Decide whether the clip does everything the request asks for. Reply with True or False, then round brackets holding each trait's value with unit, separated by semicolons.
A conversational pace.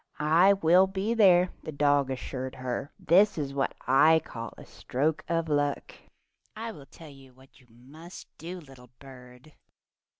True (160 wpm)